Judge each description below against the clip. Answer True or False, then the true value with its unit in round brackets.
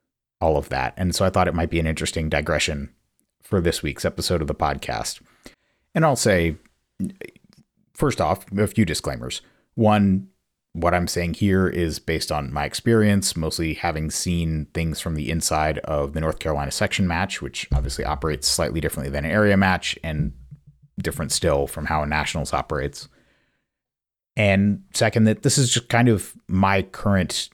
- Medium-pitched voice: False (85 Hz)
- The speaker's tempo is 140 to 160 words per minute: False (170 wpm)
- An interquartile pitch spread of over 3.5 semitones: True (4.3 semitones)